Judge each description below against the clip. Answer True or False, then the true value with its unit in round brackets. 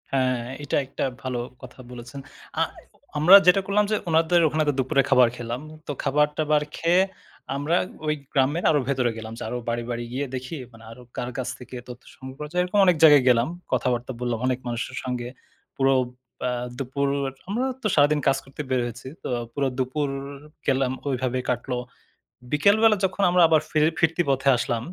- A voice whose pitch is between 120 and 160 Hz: True (135 Hz)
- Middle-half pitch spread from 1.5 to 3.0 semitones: False (3.7 semitones)